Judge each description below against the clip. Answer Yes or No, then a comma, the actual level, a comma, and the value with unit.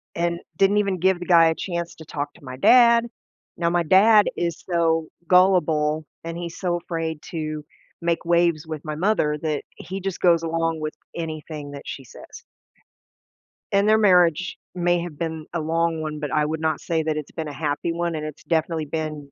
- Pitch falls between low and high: Yes, medium, 165 Hz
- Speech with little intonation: Yes, narrow, 2.2 semitones